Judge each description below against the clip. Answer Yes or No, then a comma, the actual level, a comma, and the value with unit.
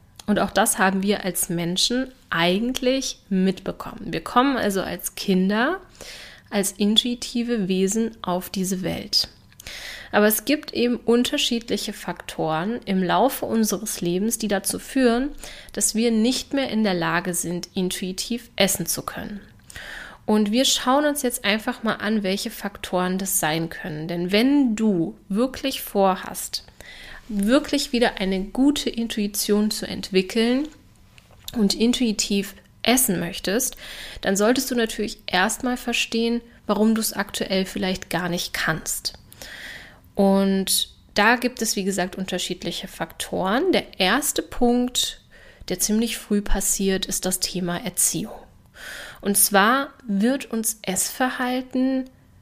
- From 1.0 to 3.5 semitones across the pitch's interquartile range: No, average, 4.2 semitones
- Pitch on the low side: No, high, 210 Hz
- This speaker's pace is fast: No, average, 130 wpm